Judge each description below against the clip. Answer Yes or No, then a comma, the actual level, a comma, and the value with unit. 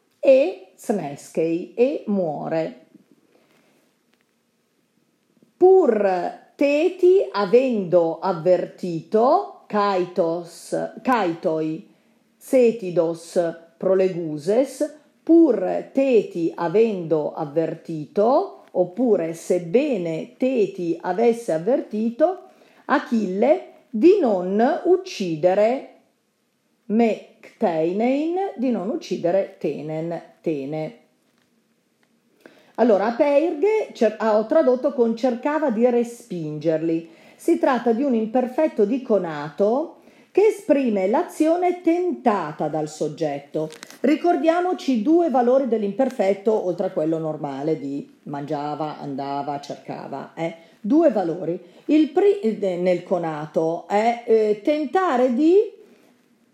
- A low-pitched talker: No, high, 220 Hz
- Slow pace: Yes, slow, 80 wpm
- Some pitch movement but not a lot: No, wide, 8.9 semitones